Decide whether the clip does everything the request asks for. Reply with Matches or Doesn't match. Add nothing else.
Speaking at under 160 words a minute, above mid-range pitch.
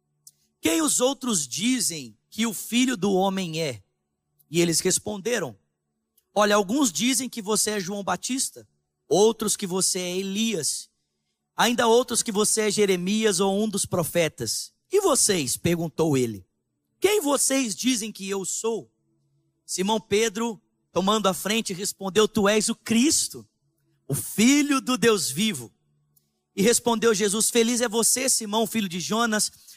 Matches